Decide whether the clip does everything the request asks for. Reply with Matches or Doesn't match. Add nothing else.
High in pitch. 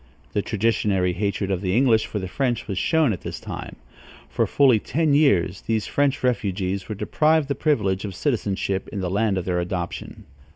Doesn't match